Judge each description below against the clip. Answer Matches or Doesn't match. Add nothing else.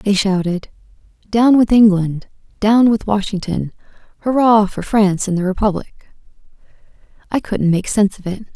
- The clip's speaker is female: Matches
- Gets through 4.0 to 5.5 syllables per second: Matches